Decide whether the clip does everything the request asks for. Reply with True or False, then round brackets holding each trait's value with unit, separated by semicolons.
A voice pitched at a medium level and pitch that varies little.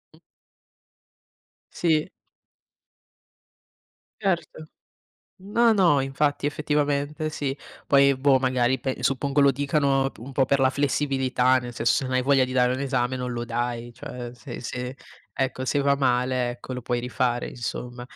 False (130 Hz; 2.3 semitones)